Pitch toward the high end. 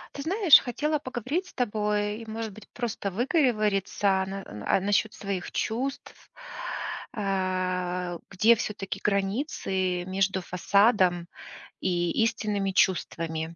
Yes: high, 200 Hz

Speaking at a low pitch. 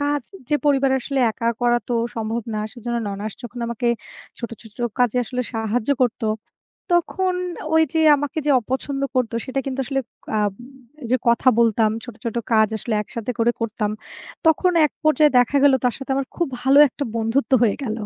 No: high, 245 Hz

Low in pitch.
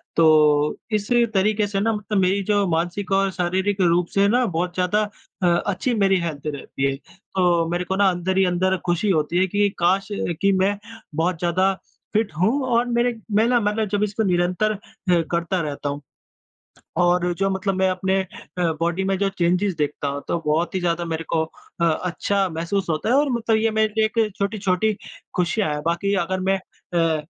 No: medium, 185 Hz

